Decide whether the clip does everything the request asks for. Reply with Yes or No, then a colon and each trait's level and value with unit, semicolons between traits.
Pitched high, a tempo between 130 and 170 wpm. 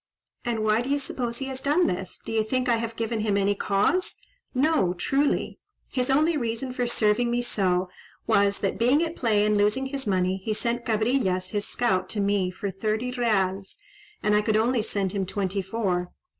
No: high, 220 Hz; average, 195 wpm